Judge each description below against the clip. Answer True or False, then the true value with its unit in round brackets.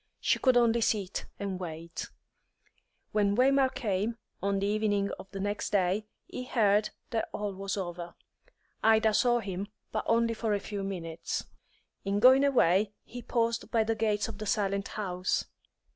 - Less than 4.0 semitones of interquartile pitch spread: True (2.7 semitones)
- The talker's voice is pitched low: False (205 Hz)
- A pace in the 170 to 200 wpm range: False (160 wpm)